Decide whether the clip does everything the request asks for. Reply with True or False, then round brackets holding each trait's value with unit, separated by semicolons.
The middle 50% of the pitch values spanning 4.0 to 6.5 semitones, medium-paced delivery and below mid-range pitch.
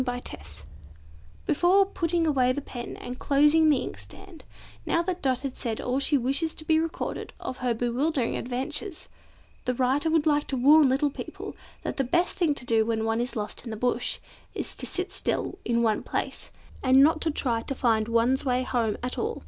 False (4.3 semitones; 195 wpm; 265 Hz)